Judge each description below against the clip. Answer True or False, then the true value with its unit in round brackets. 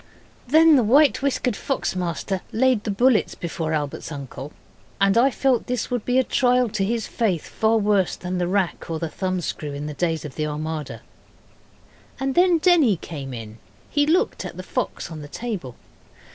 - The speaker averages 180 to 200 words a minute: True (185 wpm)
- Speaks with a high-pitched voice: True (200 Hz)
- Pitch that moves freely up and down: True (7.9 semitones)